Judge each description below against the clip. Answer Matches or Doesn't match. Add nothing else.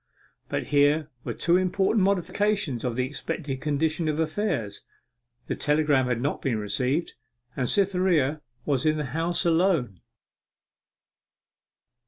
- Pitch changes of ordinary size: Matches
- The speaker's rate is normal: Doesn't match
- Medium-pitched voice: Matches